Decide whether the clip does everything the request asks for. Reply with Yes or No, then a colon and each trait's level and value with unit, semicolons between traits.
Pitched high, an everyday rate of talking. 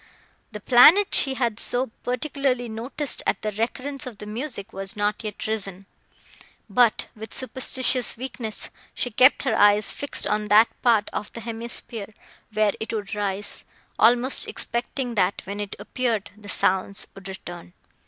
Yes: high, 220 Hz; average, 155 wpm